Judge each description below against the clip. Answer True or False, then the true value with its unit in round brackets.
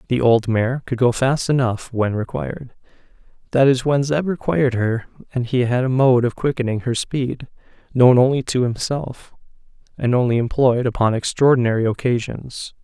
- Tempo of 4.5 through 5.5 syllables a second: True (5.0 syllables/s)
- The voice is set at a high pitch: False (125 Hz)